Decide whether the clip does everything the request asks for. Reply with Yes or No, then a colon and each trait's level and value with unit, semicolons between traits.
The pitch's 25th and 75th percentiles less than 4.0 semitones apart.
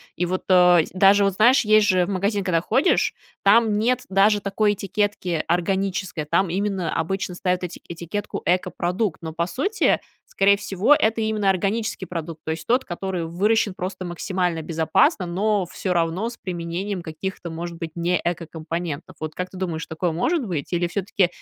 Yes: average, 3.1 semitones